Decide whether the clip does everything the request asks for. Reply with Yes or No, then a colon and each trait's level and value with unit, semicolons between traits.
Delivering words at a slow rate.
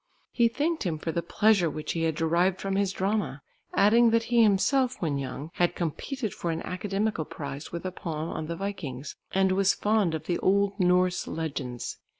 No: average, 190 wpm